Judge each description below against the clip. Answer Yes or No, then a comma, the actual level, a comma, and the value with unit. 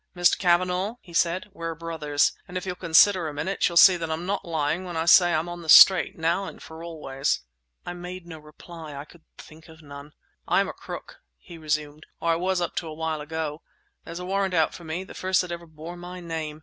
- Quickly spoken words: Yes, fast, 225 wpm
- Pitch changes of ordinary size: No, narrow, 2.2 semitones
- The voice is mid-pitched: Yes, medium, 170 Hz